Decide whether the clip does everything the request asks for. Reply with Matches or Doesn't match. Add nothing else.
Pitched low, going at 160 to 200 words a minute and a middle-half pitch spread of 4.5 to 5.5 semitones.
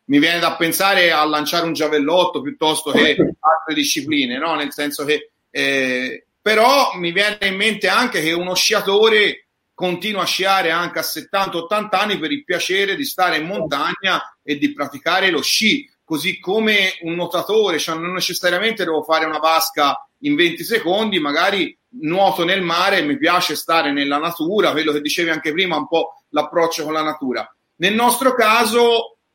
Doesn't match